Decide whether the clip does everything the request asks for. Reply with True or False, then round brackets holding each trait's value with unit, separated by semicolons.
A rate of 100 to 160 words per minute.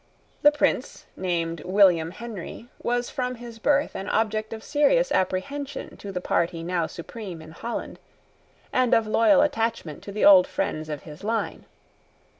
True (155 wpm)